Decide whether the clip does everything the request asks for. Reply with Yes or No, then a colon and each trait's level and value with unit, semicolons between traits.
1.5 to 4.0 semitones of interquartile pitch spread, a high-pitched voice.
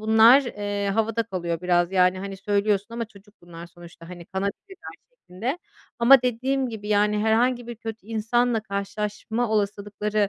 Yes: average, 2.7 semitones; high, 210 Hz